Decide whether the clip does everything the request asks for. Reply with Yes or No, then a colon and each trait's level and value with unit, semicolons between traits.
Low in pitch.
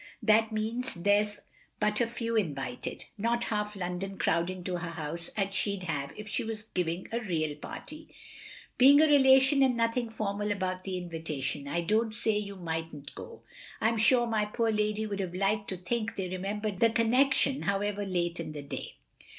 No: high, 205 Hz